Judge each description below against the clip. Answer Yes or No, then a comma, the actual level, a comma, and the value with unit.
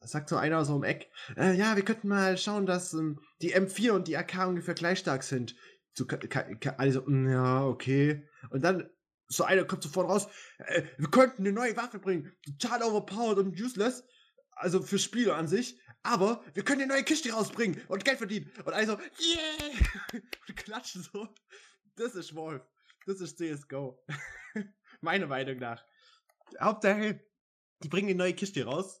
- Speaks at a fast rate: No, average, 175 wpm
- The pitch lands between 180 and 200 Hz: Yes, high, 190 Hz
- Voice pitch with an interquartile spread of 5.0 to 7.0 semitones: Yes, wide, 5.4 semitones